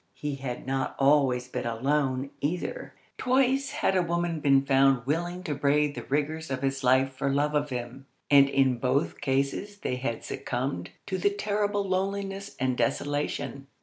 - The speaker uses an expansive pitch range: No, average, 4.6 semitones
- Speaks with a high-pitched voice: No, medium, 140 Hz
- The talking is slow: No, average, 165 wpm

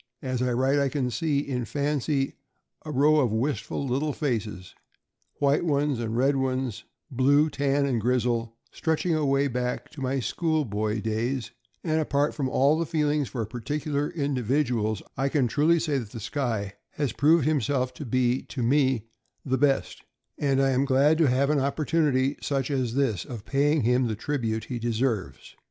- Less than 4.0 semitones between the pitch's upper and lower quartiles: Yes, average, 3.2 semitones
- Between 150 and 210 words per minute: Yes, average, 175 wpm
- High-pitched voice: No, low, 135 Hz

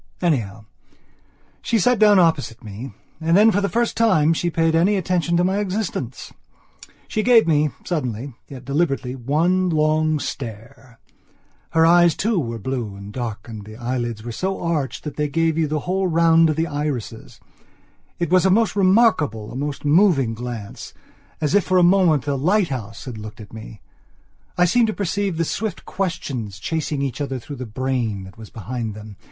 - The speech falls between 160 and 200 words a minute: Yes, average, 180 wpm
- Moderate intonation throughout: No, wide, 6.9 semitones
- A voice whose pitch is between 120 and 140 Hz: No, medium, 150 Hz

